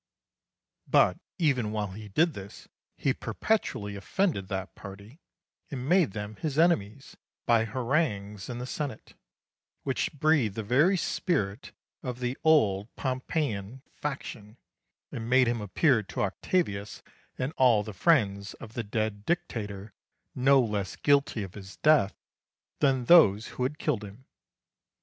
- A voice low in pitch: Yes, low, 120 Hz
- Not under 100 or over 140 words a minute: Yes, slow, 135 wpm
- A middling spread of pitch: No, wide, 5.7 semitones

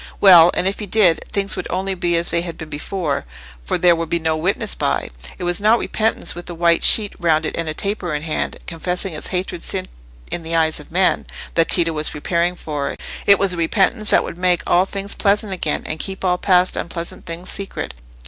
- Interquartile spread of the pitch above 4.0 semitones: No, average, 2.7 semitones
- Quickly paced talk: Yes, fast, 215 wpm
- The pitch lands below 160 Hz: No, medium, 175 Hz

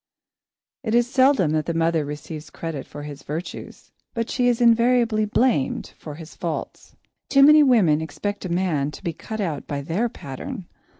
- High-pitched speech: No, medium, 175 Hz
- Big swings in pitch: Yes, wide, 7.6 semitones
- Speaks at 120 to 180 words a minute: Yes, average, 175 wpm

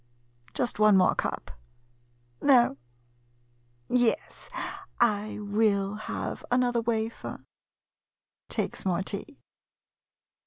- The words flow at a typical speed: No, slow, 90 wpm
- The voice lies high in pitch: Yes, high, 210 Hz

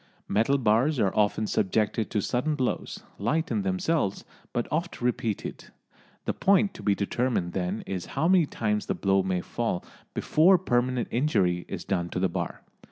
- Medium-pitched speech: No, low, 115 Hz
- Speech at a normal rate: Yes, average, 165 wpm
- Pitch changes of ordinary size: No, wide, 7.5 semitones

